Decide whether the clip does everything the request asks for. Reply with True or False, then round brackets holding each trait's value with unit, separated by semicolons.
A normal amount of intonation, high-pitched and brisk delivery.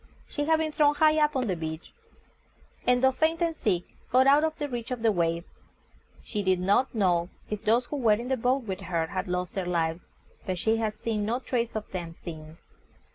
False (6.6 semitones; 220 Hz; 220 wpm)